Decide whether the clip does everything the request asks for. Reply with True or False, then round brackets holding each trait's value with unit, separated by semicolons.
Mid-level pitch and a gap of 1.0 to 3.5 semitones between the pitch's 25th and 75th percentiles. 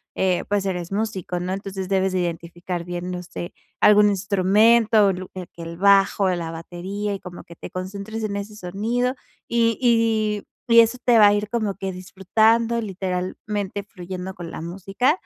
False (195 Hz; 2.9 semitones)